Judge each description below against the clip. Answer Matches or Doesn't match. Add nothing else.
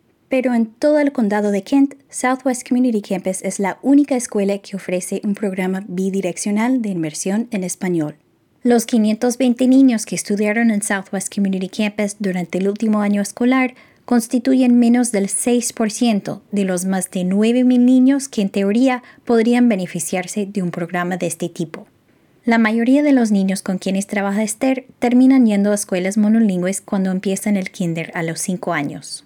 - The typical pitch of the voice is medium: Doesn't match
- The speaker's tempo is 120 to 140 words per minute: Doesn't match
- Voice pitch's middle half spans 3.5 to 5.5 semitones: Matches